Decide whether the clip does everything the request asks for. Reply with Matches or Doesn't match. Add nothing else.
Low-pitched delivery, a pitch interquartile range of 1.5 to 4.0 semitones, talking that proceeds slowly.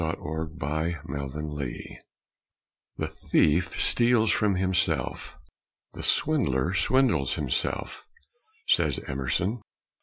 Doesn't match